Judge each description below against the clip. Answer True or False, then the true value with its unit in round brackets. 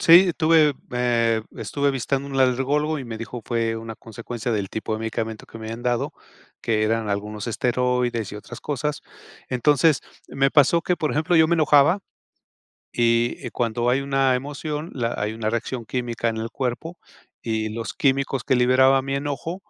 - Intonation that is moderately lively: True (3.8 semitones)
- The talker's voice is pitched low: True (125 Hz)